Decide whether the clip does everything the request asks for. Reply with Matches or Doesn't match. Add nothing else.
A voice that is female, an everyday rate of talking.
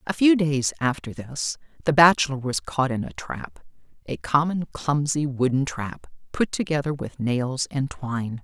Matches